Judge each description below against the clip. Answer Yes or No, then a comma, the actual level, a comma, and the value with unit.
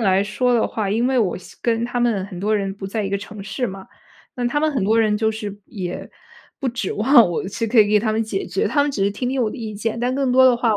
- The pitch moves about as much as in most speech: Yes, average, 3.3 semitones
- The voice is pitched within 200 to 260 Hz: Yes, high, 220 Hz